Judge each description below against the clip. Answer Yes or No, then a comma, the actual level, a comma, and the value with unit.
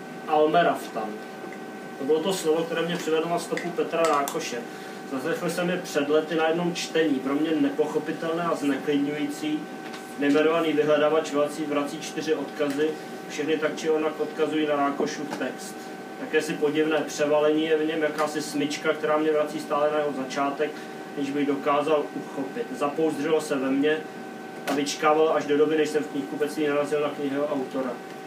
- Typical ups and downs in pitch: No, narrow, 1.3 semitones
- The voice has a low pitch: No, medium, 150 Hz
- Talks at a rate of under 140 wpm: No, average, 160 wpm